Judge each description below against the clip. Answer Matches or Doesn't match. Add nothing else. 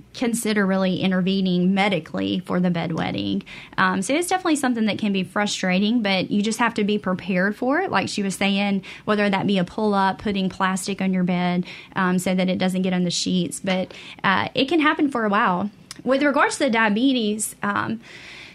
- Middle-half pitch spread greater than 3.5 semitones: Doesn't match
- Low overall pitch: Doesn't match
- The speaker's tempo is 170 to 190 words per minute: Doesn't match